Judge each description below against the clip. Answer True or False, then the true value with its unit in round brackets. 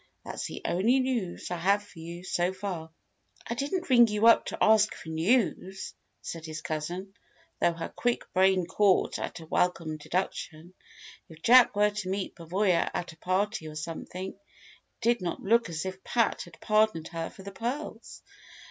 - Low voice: False (190 Hz)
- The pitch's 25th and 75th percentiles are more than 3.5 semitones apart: True (4.2 semitones)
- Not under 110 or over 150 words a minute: False (175 wpm)